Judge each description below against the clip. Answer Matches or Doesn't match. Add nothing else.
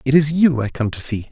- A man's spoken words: Matches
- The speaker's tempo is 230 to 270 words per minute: Doesn't match